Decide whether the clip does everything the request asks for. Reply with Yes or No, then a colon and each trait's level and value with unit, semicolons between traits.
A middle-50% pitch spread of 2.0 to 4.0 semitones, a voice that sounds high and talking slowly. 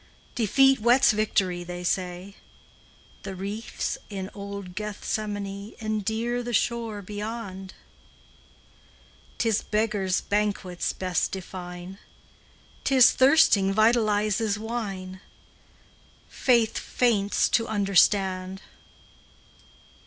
Yes: average, 2.8 semitones; high, 205 Hz; slow, 85 wpm